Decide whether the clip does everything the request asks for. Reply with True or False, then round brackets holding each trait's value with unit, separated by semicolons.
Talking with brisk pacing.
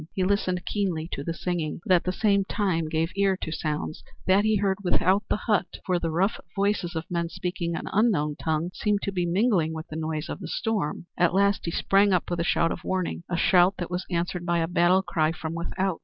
True (230 wpm)